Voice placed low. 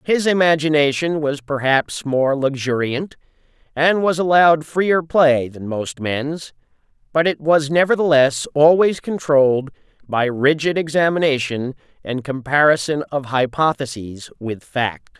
No: medium, 145 Hz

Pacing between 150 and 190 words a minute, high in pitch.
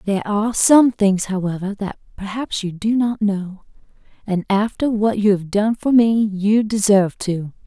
Yes: average, 170 wpm; high, 205 Hz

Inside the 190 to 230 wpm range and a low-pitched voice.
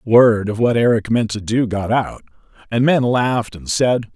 Yes: average, 200 wpm; low, 115 Hz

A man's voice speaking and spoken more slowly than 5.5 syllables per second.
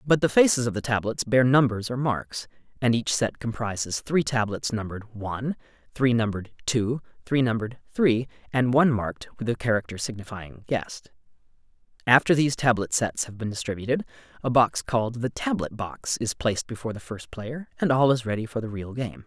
No: male; 5.6 syllables/s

